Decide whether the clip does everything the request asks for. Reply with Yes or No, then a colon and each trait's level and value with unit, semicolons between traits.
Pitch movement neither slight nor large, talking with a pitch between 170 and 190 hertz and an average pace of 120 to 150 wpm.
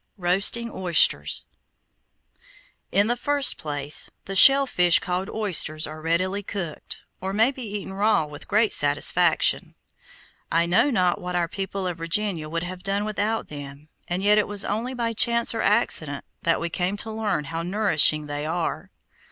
No: average, 4.3 semitones; medium, 185 Hz; average, 165 wpm